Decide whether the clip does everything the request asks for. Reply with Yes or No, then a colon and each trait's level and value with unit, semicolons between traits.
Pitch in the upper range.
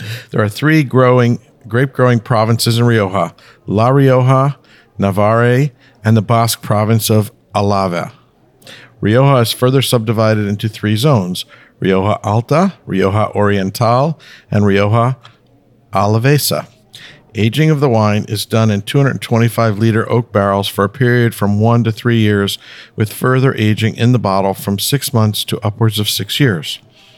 No: low, 115 Hz